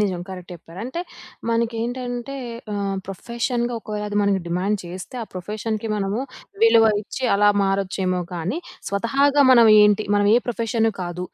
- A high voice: Yes, high, 210 Hz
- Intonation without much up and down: No, average, 3.4 semitones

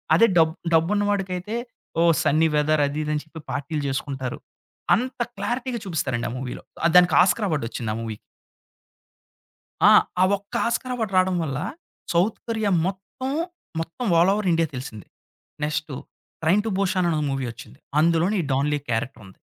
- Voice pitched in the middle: Yes, medium, 165 Hz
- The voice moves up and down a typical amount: No, wide, 5.9 semitones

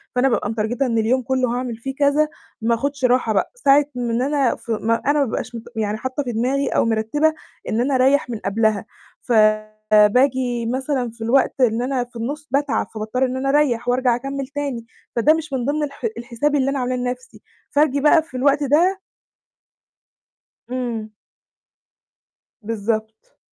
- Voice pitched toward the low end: No, very high, 250 Hz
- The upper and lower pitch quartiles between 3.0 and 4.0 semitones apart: Yes, average, 3.5 semitones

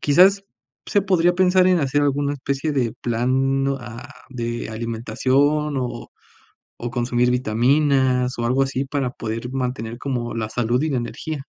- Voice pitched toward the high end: No, low, 130 Hz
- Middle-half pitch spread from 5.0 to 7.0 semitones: No, average, 3.2 semitones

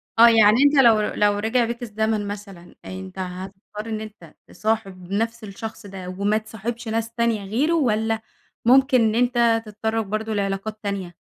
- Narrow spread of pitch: Yes, narrow, 2.2 semitones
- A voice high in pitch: Yes, high, 220 Hz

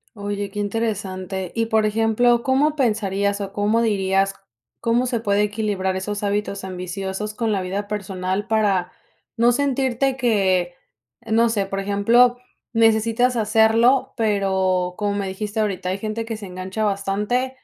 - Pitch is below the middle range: No, high, 210 Hz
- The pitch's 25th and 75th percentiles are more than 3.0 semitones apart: No, average, 2.7 semitones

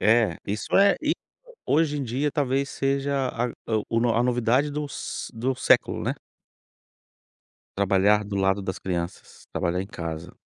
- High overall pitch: No, low, 120 Hz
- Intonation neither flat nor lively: No, wide, 5.8 semitones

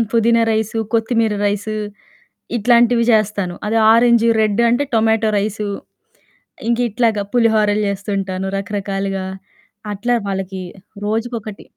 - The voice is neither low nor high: No, high, 215 Hz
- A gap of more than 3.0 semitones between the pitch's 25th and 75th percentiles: No, narrow, 2.4 semitones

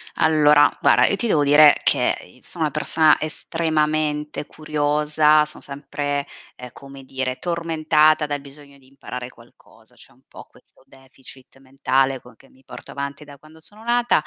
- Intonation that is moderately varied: No, narrow, 2.3 semitones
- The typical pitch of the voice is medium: Yes, medium, 145 Hz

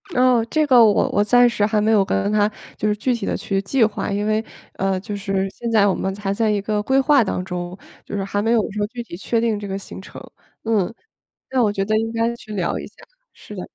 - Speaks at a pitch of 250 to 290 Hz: No, high, 210 Hz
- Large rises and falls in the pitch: No, narrow, 2.6 semitones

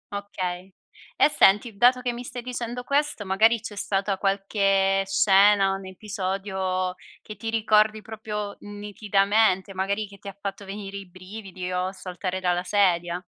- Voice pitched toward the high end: Yes, high, 200 Hz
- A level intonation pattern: Yes, narrow, 2.0 semitones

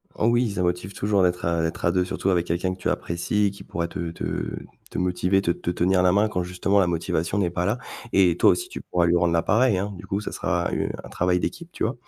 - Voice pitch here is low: Yes, very low, 90 Hz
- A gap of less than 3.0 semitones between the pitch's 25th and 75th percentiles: Yes, narrow, 2.4 semitones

